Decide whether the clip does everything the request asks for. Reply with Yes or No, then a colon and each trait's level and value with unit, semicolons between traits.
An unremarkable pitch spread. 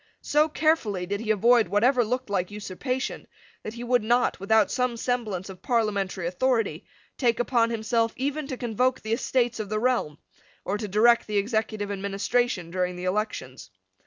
Yes: average, 3.5 semitones